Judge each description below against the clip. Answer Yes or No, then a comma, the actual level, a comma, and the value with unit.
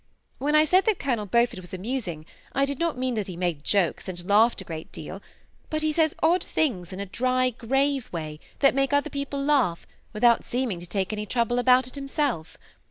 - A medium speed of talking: No, fast, 210 wpm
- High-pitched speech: Yes, high, 245 Hz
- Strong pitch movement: Yes, wide, 6.8 semitones